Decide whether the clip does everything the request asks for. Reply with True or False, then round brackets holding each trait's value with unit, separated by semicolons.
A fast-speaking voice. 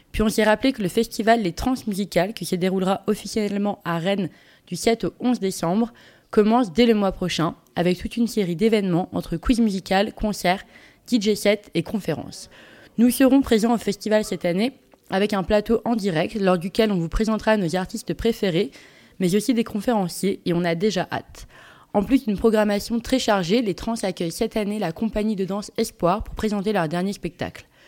False (190 wpm)